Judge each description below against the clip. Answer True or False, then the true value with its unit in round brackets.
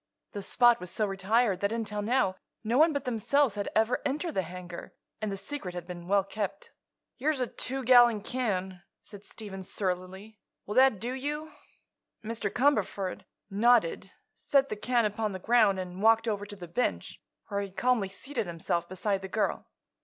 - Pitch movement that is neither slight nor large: True (4.2 semitones)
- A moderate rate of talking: True (175 wpm)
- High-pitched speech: True (210 Hz)